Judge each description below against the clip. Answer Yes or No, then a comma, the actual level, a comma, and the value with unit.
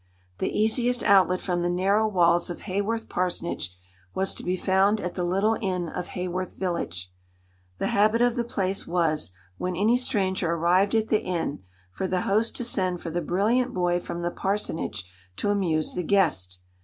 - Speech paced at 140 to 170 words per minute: No, average, 180 wpm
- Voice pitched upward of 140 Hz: Yes, medium, 185 Hz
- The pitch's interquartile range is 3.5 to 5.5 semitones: No, average, 2.9 semitones